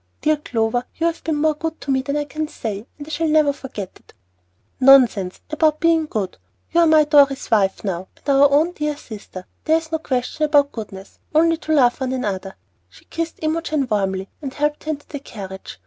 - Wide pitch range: Yes, wide, 5.7 semitones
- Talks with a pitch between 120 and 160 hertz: No, very high, 285 Hz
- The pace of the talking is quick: Yes, fast, 210 wpm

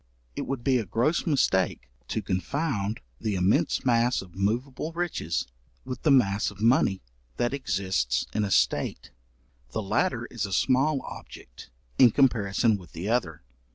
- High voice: No, low, 110 Hz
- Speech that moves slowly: No, average, 155 wpm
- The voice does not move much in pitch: No, average, 5.3 semitones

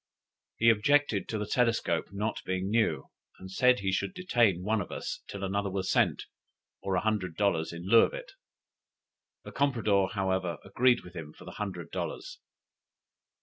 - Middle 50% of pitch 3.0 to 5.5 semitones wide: Yes, average, 3.7 semitones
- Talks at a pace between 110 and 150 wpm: No, average, 170 wpm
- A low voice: Yes, low, 100 Hz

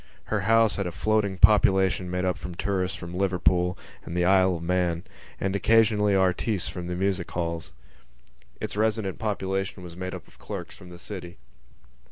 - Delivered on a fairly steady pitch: Yes, narrow, 2.2 semitones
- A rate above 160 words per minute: Yes, average, 175 wpm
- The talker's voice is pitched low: Yes, very low, 95 Hz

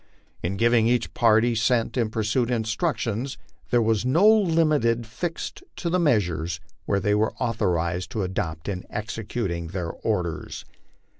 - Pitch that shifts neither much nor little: Yes, average, 4.3 semitones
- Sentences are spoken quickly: No, average, 140 wpm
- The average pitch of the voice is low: Yes, low, 110 Hz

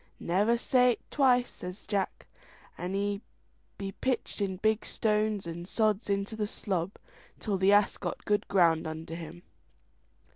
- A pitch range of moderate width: Yes, average, 3.2 semitones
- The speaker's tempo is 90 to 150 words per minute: Yes, average, 140 wpm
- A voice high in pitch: Yes, high, 200 Hz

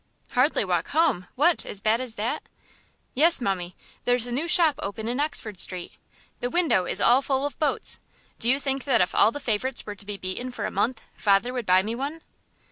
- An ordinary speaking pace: No, fast, 210 wpm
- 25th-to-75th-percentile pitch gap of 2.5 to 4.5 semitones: No, average, 5.3 semitones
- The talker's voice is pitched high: Yes, high, 245 Hz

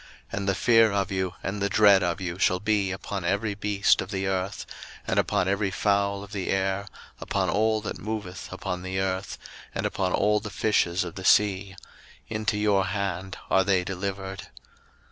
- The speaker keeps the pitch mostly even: Yes, narrow, 1.5 semitones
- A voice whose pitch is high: No, low, 100 Hz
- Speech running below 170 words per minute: No, average, 185 wpm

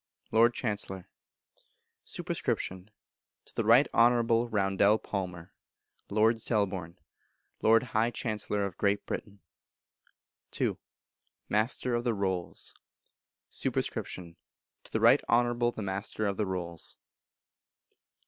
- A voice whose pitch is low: Yes, low, 105 Hz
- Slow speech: Yes, slow, 105 wpm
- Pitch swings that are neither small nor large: Yes, average, 3.3 semitones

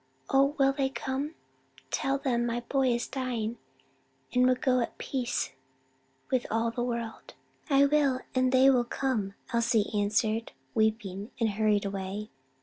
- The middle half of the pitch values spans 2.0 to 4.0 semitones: Yes, average, 3.3 semitones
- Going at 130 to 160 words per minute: Yes, average, 145 wpm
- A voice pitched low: No, high, 240 Hz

